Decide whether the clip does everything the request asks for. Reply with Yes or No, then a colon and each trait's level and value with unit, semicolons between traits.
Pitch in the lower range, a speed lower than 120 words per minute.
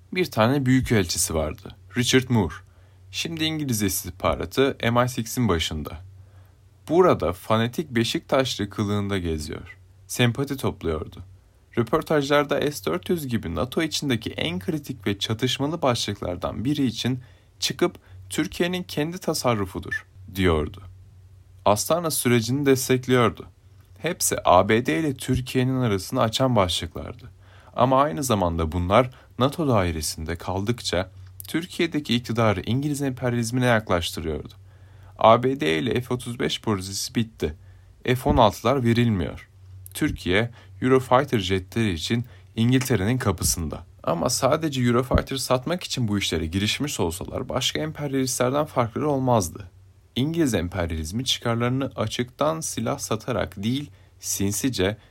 Yes: low, 115 Hz; average, 100 wpm